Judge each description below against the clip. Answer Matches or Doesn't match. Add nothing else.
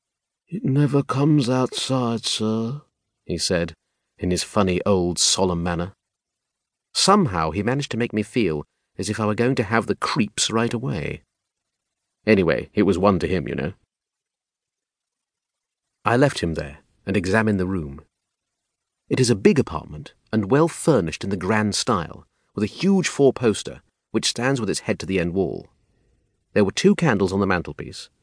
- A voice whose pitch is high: Doesn't match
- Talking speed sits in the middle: Matches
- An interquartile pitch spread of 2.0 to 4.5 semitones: Doesn't match